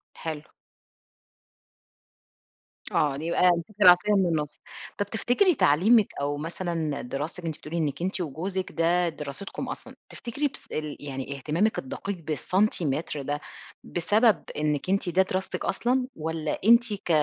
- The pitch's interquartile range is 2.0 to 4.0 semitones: No, average, 5.0 semitones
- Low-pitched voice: No, medium, 170 Hz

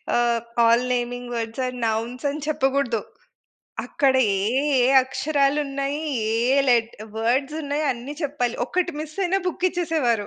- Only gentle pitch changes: No, average, 3.7 semitones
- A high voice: Yes, very high, 265 Hz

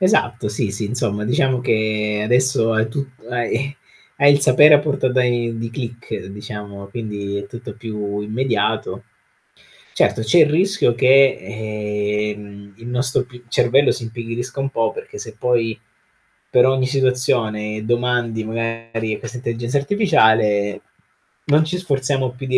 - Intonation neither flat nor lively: Yes, average, 3.3 semitones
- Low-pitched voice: Yes, low, 120 Hz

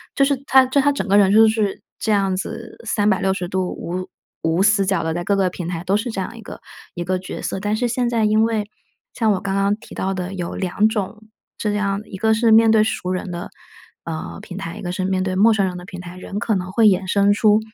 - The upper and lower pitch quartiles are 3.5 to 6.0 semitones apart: No, average, 2.8 semitones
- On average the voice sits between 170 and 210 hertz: Yes, high, 195 Hz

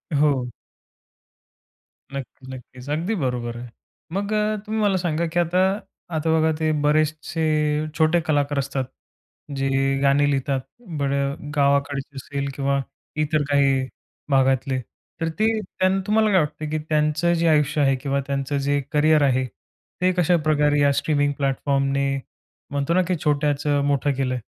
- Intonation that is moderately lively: No, narrow, 2.3 semitones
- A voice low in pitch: No, medium, 145 Hz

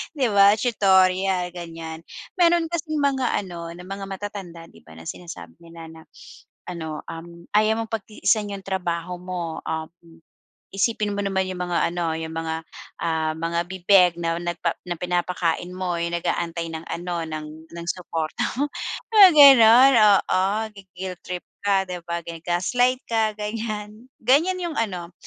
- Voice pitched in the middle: Yes, medium, 180 Hz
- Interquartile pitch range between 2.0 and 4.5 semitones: Yes, average, 3.8 semitones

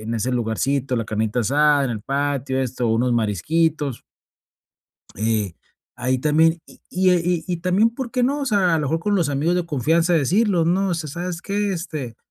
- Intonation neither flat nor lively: No, wide, 6.1 semitones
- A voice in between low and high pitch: Yes, medium, 150 Hz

